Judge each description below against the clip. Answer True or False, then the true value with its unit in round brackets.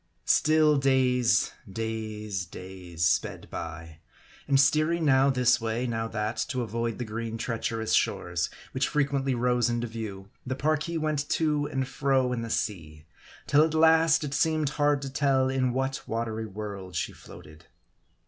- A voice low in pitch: True (125 Hz)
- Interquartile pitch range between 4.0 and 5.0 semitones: True (4.3 semitones)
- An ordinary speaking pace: True (160 wpm)